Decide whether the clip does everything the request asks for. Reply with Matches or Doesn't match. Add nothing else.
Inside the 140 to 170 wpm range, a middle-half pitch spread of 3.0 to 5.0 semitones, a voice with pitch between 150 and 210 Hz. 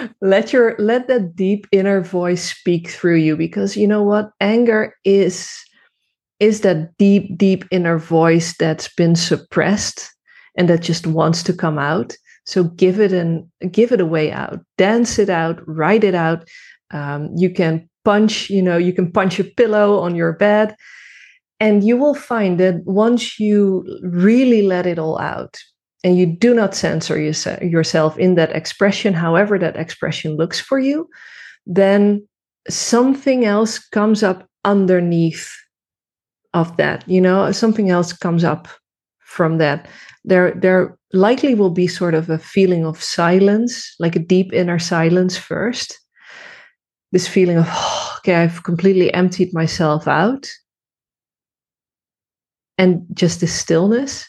Matches